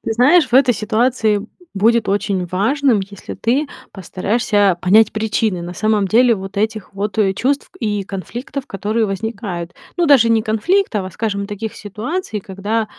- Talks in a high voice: Yes, high, 215 Hz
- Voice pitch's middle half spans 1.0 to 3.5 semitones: Yes, average, 2.9 semitones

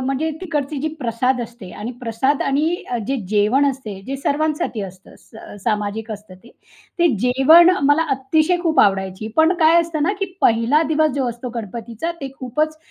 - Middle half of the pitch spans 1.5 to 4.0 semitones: No, wide, 5.5 semitones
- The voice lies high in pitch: Yes, very high, 265 Hz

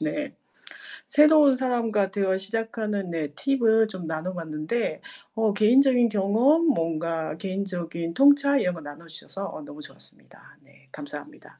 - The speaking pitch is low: No, high, 200 Hz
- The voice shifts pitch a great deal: Yes, wide, 6.7 semitones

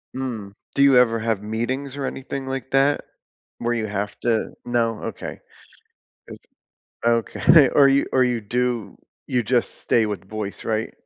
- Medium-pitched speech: No, low, 120 Hz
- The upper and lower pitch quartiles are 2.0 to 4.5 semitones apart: Yes, average, 3.4 semitones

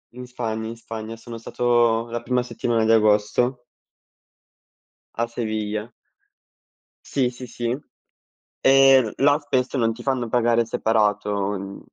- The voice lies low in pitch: Yes, low, 115 Hz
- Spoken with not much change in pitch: Yes, narrow, 1.9 semitones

